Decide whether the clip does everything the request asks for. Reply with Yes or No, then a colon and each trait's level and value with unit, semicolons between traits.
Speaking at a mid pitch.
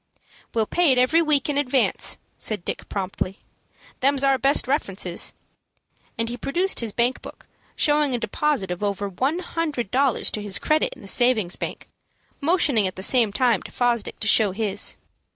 No: high, 245 Hz